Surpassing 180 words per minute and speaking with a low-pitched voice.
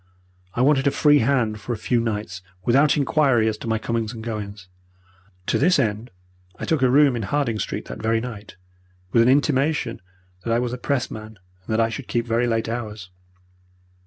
Yes: average, 195 wpm; low, 115 Hz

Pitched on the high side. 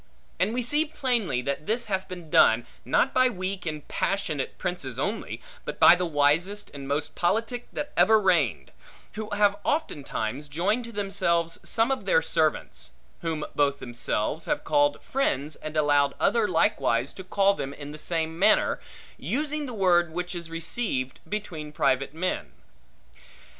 No: medium, 180 Hz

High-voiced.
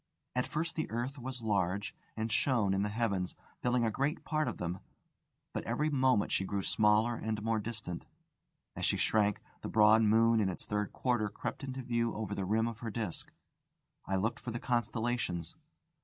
No: low, 110 Hz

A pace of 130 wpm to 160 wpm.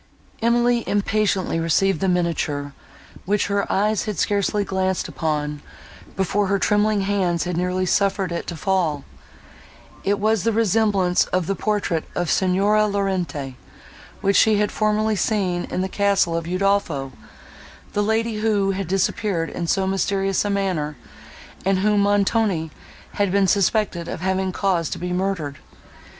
Yes: average, 140 wpm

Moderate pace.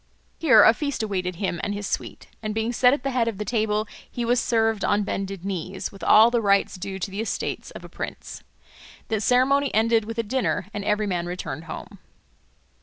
No: fast, 210 wpm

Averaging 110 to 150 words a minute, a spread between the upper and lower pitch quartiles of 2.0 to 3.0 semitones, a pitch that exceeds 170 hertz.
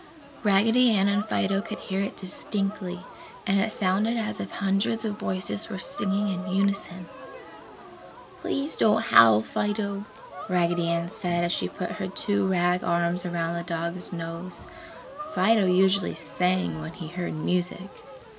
Yes: average, 145 wpm; average, 2.7 semitones; high, 190 Hz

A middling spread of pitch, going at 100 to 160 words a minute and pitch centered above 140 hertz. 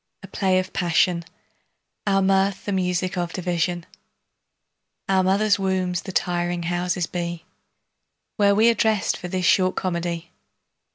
No: narrow, 1.7 semitones; slow, 135 wpm; medium, 185 Hz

